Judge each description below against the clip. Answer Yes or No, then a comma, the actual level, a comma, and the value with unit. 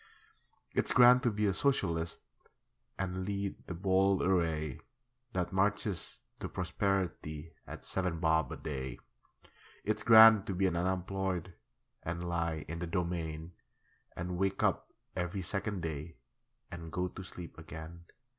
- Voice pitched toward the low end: Yes, very low, 90 Hz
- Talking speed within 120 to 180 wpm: Yes, slow, 135 wpm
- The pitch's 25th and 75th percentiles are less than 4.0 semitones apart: Yes, average, 2.7 semitones